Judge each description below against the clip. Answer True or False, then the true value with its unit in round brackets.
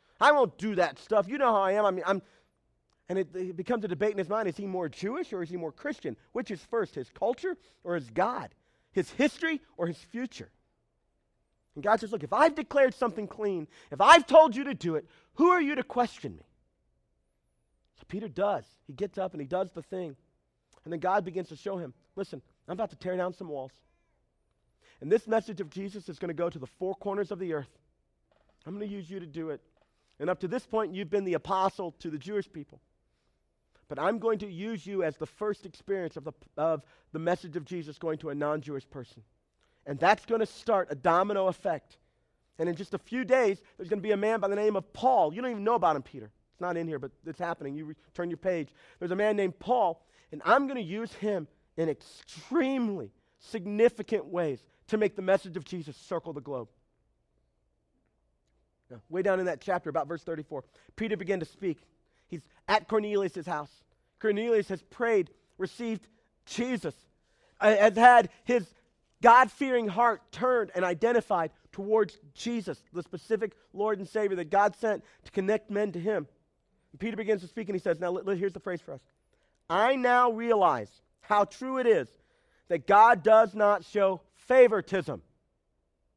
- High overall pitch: True (195 Hz)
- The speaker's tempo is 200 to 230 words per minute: True (205 wpm)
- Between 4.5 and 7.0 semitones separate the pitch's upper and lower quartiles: True (4.9 semitones)